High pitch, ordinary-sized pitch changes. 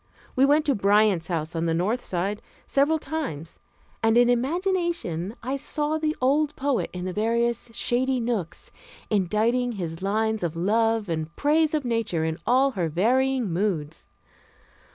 No: high, 225 Hz; wide, 6.9 semitones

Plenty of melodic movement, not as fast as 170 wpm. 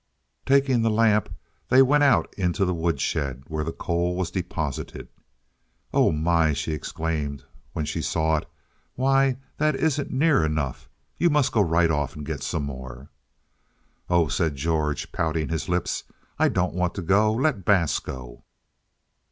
Yes: wide, 6.0 semitones; average, 155 wpm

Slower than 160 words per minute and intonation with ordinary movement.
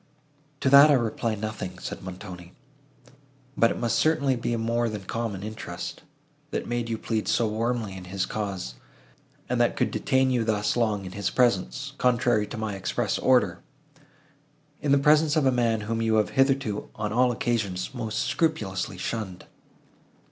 No: average, 165 wpm; average, 4.2 semitones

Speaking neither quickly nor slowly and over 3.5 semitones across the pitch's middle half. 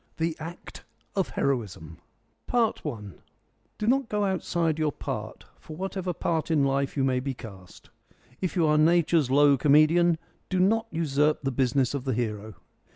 Yes: average, 160 wpm; average, 4.4 semitones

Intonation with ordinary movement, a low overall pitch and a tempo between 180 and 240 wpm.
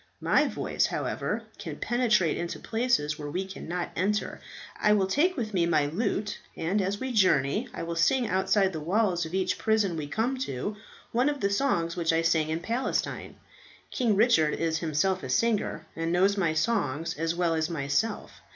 No: average, 5.0 semitones; medium, 185 Hz; average, 185 wpm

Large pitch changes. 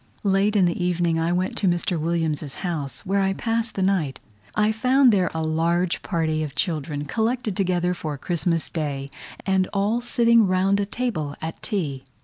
No: average, 4.0 semitones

